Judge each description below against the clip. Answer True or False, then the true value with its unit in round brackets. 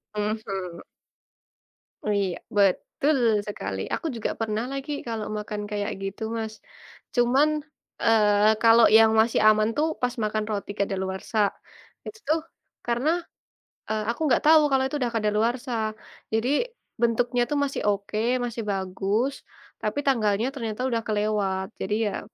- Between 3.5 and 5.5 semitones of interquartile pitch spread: False (2.7 semitones)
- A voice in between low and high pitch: False (220 Hz)